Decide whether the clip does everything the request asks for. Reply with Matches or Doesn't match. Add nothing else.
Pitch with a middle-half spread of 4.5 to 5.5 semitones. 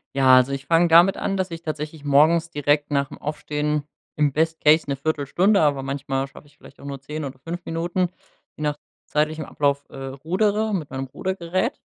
Doesn't match